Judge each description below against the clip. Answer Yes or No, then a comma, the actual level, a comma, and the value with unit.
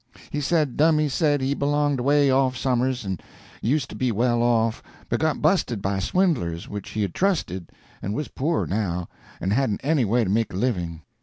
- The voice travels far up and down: Yes, wide, 6.1 semitones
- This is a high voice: No, low, 125 Hz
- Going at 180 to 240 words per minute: Yes, average, 190 wpm